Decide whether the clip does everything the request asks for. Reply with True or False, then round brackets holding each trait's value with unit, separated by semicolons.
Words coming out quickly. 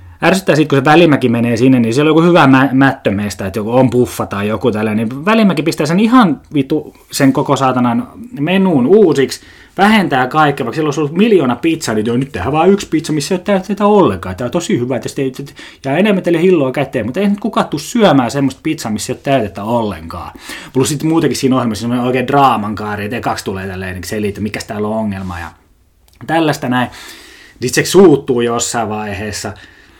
True (205 wpm)